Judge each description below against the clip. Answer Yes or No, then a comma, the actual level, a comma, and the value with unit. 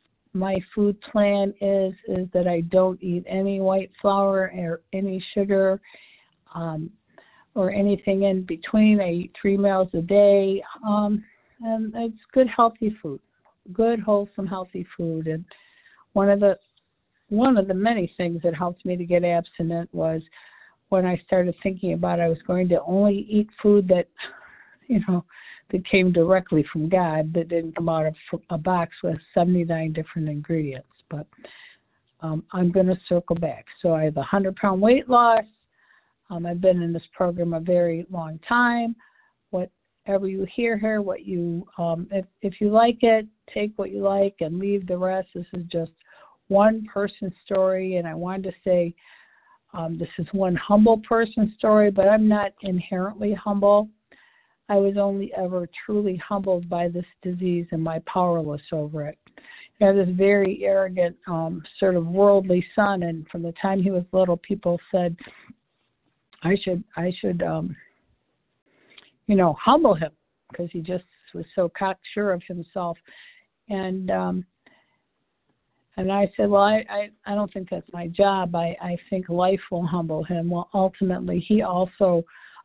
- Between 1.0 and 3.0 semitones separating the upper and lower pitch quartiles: Yes, average, 2.7 semitones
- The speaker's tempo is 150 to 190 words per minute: Yes, average, 165 wpm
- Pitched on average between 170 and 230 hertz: Yes, medium, 185 Hz